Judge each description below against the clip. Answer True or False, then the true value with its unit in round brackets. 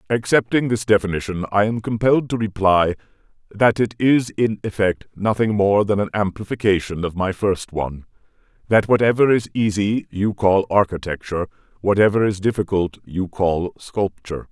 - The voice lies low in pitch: True (105 Hz)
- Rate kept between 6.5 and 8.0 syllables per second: False (5.1 syllables/s)